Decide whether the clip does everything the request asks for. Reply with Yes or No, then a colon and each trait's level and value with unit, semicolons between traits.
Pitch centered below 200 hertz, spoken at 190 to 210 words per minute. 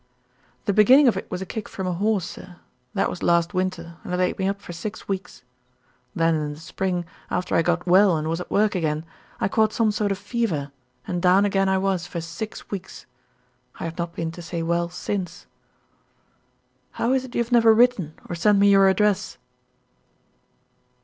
Yes: medium, 185 Hz; average, 200 wpm